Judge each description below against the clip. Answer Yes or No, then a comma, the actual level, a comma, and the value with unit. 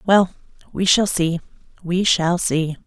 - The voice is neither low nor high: Yes, medium, 175 Hz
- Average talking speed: Yes, average, 145 wpm